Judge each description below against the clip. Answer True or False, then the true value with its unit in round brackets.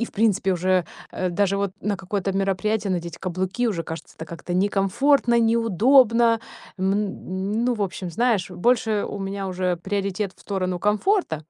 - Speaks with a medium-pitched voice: False (195 Hz)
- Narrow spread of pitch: False (3.2 semitones)